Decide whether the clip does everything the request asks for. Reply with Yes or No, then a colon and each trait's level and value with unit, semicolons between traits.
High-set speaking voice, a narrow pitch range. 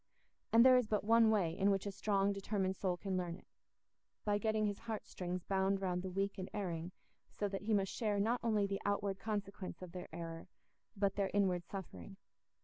Yes: high, 195 Hz; narrow, 2.0 semitones